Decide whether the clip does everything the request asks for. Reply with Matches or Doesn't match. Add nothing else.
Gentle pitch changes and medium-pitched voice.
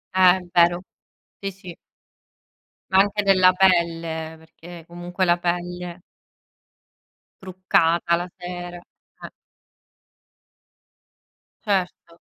Matches